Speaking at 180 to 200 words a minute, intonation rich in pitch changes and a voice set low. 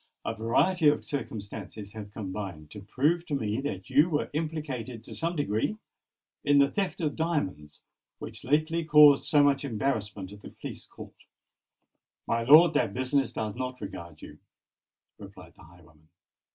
No: average, 155 wpm; wide, 6.7 semitones; low, 125 Hz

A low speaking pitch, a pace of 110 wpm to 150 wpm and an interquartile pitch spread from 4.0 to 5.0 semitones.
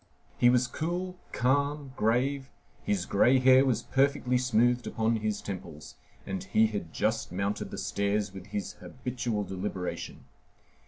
Yes: low, 115 Hz; average, 140 wpm; average, 4.4 semitones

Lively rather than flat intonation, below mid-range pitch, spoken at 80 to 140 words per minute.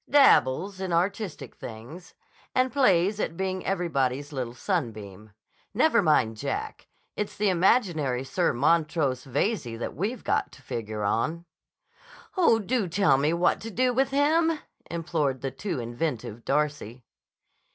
No: wide, 7.7 semitones; medium, 165 Hz; slow, 135 wpm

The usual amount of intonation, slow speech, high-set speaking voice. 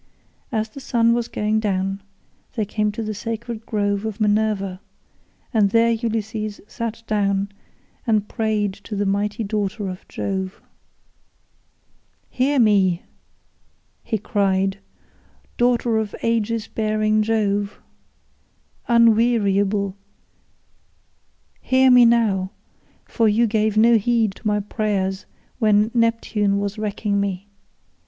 No: narrow, 2.2 semitones; slow, 115 wpm; high, 215 Hz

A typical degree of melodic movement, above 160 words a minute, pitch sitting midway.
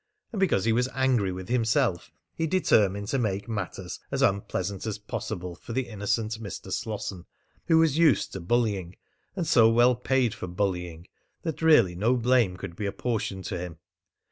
No: average, 4.8 semitones; average, 170 wpm; low, 110 Hz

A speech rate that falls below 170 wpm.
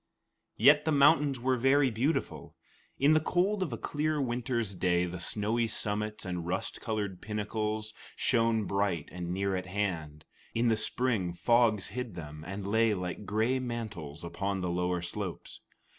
Yes: average, 160 wpm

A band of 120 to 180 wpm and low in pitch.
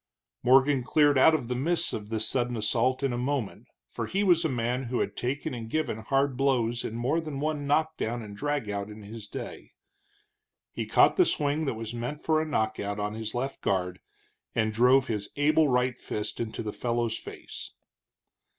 No: average, 200 wpm; low, 125 Hz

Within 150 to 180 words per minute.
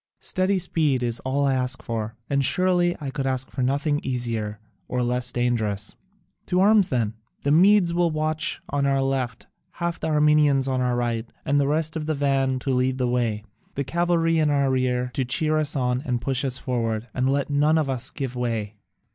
No: average, 200 wpm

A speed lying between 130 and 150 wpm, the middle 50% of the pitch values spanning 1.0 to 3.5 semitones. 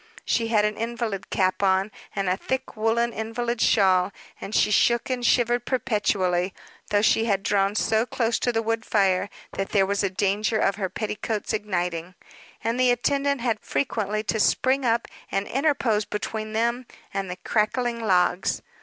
No: average, 170 wpm; average, 3.2 semitones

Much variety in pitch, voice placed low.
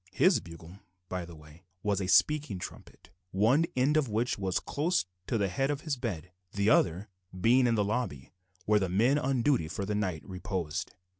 Yes: wide, 5.8 semitones; low, 105 Hz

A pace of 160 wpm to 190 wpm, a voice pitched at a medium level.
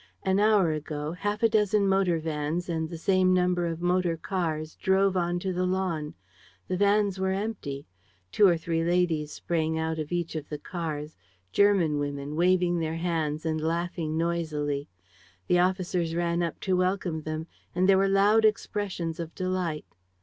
Yes: average, 165 wpm; medium, 175 Hz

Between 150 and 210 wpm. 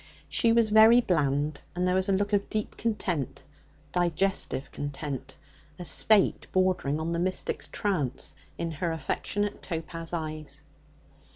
No: slow, 135 wpm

